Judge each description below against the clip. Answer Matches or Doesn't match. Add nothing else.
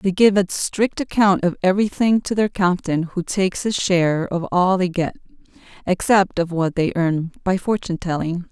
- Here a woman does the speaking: Matches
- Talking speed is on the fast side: Doesn't match